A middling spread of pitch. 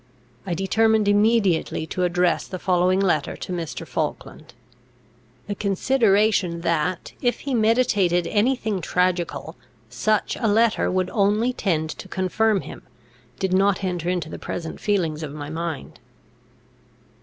Yes: average, 3.8 semitones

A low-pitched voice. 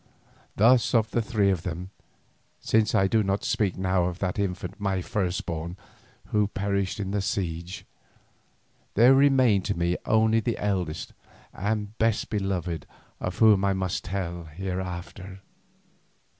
Yes: very low, 95 Hz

